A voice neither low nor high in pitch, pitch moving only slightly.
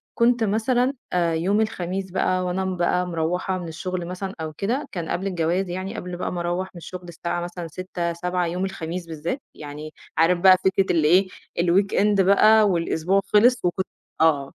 Yes: medium, 180 Hz; narrow, 2.2 semitones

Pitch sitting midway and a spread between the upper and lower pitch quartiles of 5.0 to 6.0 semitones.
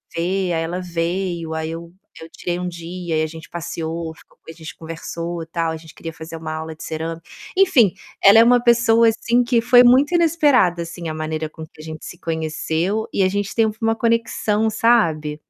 Yes: medium, 170 Hz; wide, 5.6 semitones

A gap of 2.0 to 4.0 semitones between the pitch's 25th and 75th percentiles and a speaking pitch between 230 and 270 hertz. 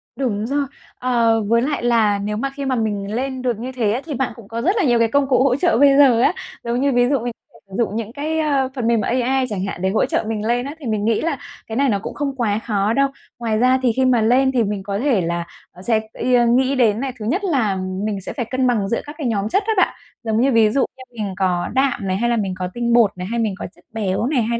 Yes: average, 3.6 semitones; high, 235 Hz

